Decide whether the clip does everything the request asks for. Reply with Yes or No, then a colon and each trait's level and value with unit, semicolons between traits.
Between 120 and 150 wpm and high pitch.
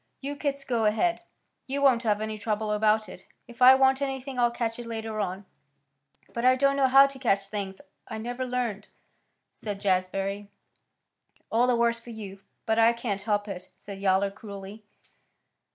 No: average, 175 wpm; high, 225 Hz